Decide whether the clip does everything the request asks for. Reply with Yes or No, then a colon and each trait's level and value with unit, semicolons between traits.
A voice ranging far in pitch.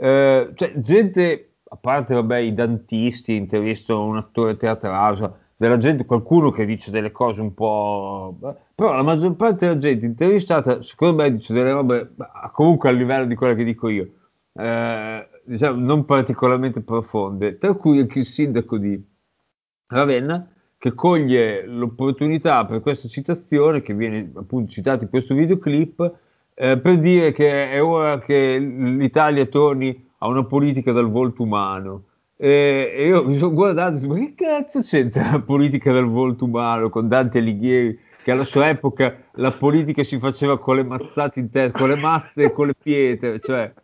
No: average, 4.0 semitones